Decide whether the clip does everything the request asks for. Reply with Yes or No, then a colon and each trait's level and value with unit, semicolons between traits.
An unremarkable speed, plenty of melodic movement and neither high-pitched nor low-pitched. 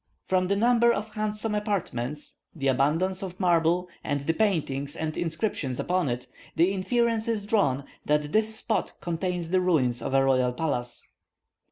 Yes: average, 160 wpm; wide, 6.7 semitones; medium, 175 Hz